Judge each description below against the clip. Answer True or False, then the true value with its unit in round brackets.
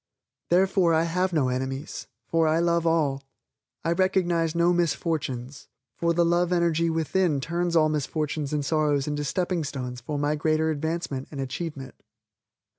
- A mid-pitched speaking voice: True (160 Hz)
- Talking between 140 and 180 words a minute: True (150 wpm)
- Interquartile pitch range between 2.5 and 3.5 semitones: True (2.8 semitones)